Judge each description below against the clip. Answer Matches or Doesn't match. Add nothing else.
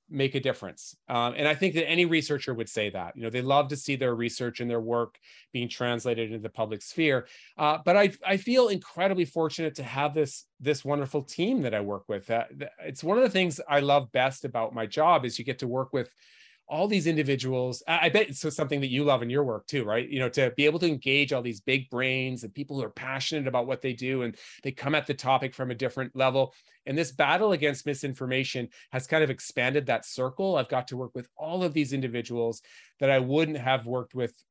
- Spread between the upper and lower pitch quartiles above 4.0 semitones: Doesn't match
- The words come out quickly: Matches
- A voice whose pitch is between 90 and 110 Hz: Doesn't match